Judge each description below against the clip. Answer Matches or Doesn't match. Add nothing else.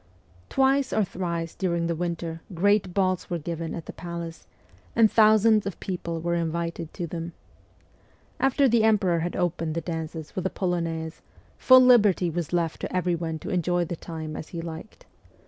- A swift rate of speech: Doesn't match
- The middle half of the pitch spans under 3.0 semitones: Matches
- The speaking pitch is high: Doesn't match